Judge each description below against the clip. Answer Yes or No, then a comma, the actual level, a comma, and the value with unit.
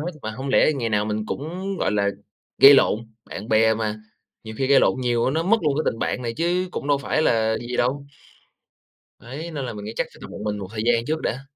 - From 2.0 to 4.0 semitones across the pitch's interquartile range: No, average, 4.9 semitones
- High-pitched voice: No, low, 125 Hz